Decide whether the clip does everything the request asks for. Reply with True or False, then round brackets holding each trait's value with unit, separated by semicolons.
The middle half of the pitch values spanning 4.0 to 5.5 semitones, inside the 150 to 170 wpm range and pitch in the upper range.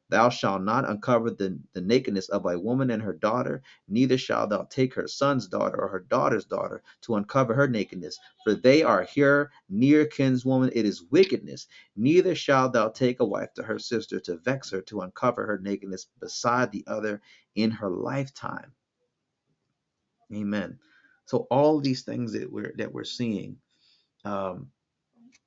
False (4.9 semitones; 165 wpm; 125 Hz)